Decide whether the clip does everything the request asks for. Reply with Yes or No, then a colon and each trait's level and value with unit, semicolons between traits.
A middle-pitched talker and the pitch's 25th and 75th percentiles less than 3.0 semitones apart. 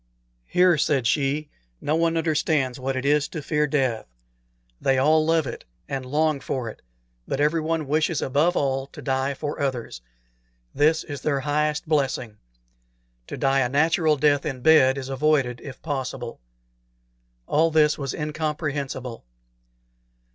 Yes: medium, 145 Hz; narrow, 2.6 semitones